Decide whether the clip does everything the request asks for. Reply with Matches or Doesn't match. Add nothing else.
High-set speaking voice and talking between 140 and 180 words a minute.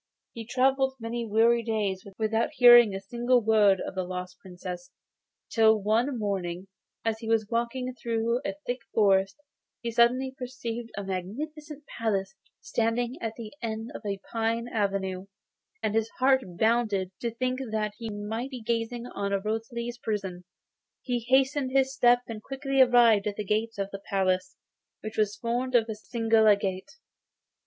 Matches